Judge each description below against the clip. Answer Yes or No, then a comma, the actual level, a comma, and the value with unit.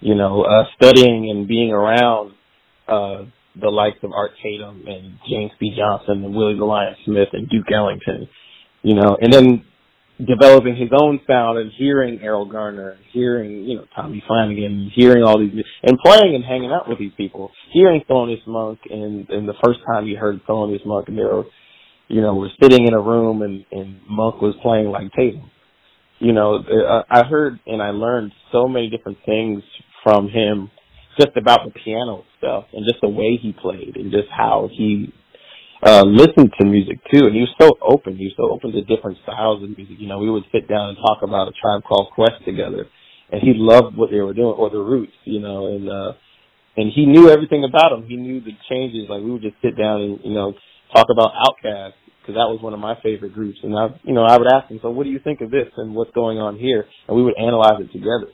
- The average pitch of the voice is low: Yes, low, 110 Hz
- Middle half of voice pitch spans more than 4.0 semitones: No, average, 2.8 semitones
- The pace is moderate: No, fast, 220 wpm